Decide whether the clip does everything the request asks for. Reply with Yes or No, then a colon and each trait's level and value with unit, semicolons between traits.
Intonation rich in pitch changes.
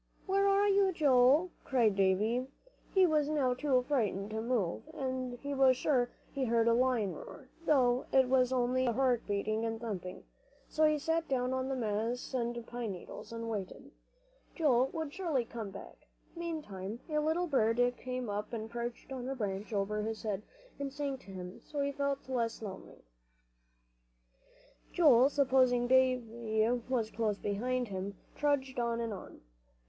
No: average, 3.8 semitones